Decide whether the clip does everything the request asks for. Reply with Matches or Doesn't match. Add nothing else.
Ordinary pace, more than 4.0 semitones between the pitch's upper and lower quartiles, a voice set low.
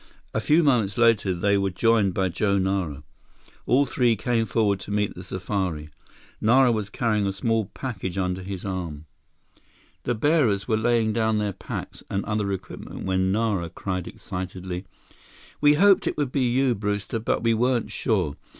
Doesn't match